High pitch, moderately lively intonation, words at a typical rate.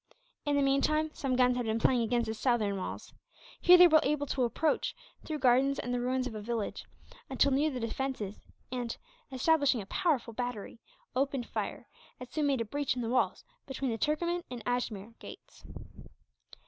Yes: very high, 255 Hz; average, 3.4 semitones; average, 185 wpm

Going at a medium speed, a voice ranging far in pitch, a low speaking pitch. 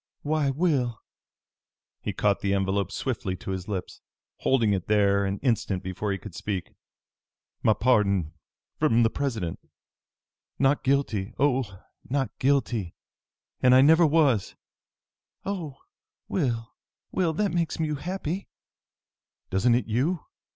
No: slow, 125 wpm; wide, 6.4 semitones; low, 120 Hz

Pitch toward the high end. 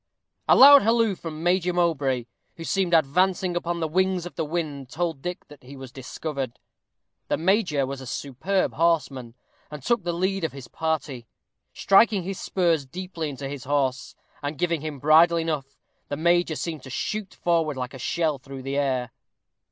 No: medium, 160 Hz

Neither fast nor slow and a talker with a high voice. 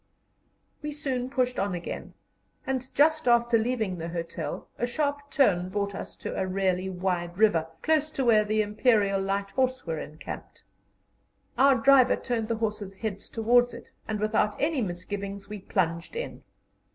Yes: average, 160 wpm; high, 215 Hz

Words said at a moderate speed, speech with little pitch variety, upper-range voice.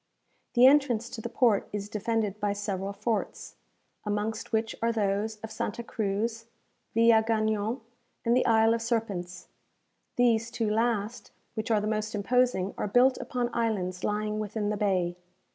Yes: average, 150 wpm; narrow, 2.0 semitones; high, 220 Hz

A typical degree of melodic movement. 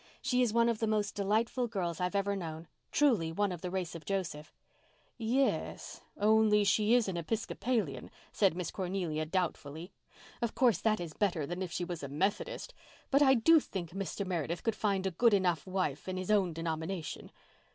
Yes: average, 4.3 semitones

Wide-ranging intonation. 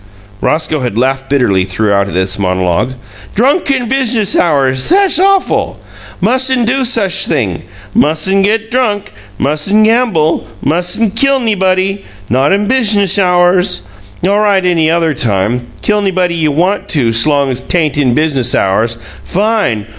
Yes: wide, 8.4 semitones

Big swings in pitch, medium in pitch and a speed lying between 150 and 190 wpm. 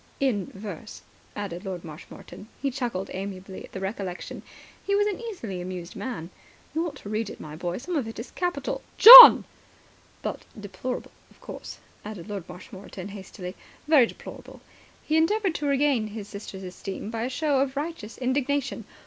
No: wide, 6.8 semitones; high, 220 Hz; average, 170 wpm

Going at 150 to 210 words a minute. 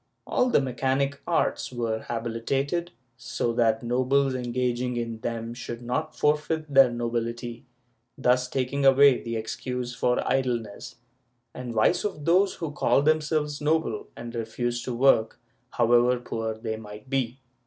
No: average, 140 wpm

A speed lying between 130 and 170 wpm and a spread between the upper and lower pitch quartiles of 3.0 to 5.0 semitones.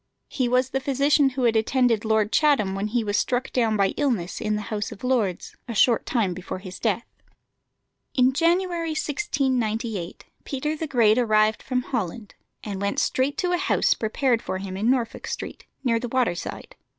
No: average, 185 wpm; average, 4.0 semitones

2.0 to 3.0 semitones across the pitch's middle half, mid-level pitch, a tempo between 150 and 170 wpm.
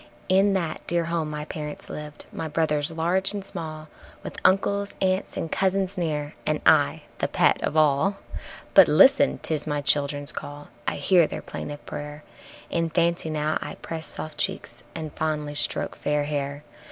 Yes: average, 2.7 semitones; medium, 155 Hz; average, 165 wpm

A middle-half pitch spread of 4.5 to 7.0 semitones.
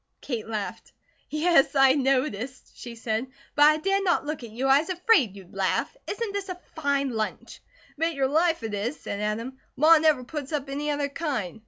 Yes: average, 5.2 semitones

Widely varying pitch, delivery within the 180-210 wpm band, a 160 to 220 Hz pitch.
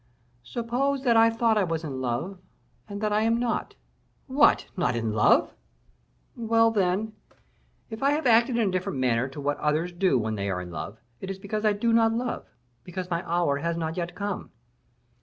Yes: wide, 7.8 semitones; average, 200 wpm; high, 190 Hz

